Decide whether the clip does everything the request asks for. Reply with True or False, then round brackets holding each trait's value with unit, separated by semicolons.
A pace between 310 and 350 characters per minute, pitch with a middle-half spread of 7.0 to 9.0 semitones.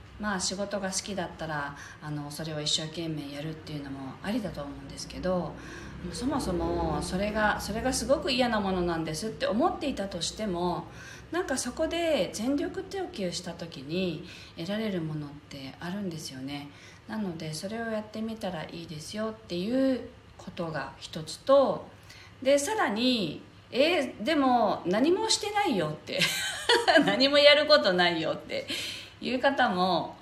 True (315 characters per minute; 8.4 semitones)